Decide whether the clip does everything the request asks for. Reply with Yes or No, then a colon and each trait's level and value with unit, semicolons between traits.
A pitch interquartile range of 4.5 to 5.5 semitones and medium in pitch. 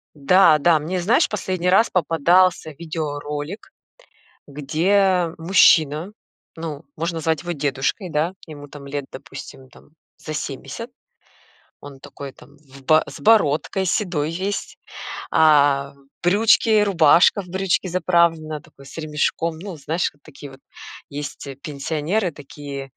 No: average, 3.9 semitones; medium, 160 Hz